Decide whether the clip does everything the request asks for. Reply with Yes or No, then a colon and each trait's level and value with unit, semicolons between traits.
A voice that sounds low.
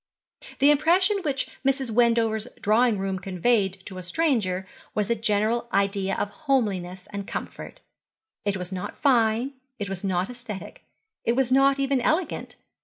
No: high, 220 Hz